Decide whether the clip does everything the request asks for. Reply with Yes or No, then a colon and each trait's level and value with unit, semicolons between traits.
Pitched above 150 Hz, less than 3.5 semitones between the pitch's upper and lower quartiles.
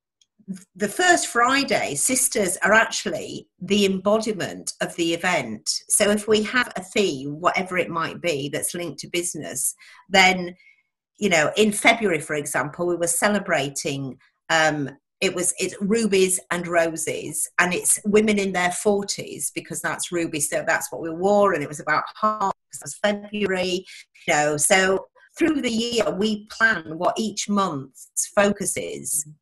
No: high, 190 Hz; average, 4.2 semitones